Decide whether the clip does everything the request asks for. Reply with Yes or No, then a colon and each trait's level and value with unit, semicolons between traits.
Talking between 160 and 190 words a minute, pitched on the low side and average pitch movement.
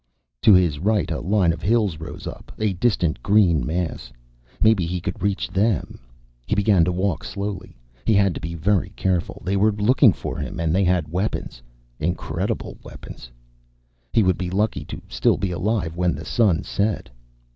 Yes: average, 180 wpm; very low, 95 Hz; average, 3.4 semitones